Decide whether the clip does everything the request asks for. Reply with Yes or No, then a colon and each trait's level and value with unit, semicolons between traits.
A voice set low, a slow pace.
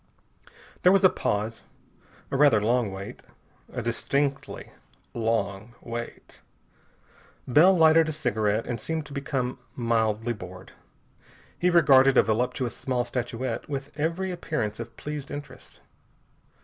Yes: low, 125 Hz; slow, 125 wpm